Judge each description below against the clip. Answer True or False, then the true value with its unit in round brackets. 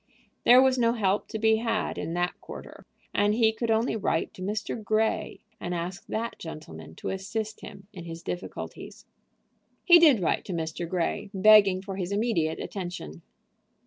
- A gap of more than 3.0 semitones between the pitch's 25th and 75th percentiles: True (4.0 semitones)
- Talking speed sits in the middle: True (170 wpm)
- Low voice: False (200 Hz)